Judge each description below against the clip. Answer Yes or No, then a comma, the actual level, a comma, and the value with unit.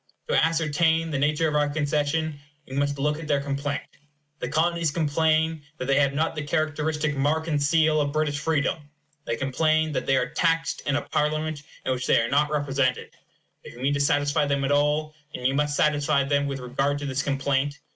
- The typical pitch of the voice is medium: Yes, medium, 145 Hz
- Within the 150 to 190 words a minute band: No, average, 200 wpm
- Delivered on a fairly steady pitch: Yes, narrow, 1.8 semitones